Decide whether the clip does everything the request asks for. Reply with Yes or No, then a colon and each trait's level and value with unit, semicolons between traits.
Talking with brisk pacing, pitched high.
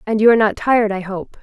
Yes: fast, 250 wpm; high, 215 Hz